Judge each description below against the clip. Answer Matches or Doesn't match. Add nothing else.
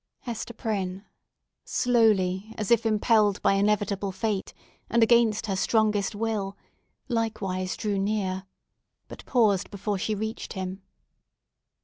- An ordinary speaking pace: Doesn't match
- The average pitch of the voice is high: Matches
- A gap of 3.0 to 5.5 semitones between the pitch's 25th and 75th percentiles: Doesn't match